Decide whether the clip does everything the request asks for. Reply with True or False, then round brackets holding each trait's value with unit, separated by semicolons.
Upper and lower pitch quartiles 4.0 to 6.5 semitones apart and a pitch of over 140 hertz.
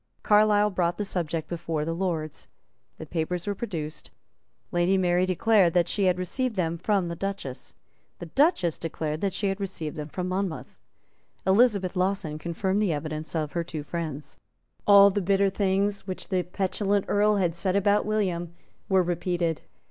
False (3.1 semitones; 185 Hz)